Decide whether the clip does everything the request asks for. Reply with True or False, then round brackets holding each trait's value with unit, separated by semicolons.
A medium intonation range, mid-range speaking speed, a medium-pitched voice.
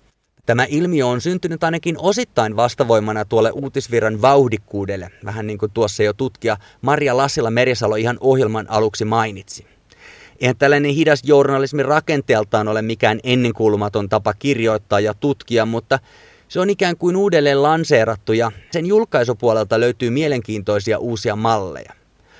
False (4.7 semitones; 130 wpm; 120 Hz)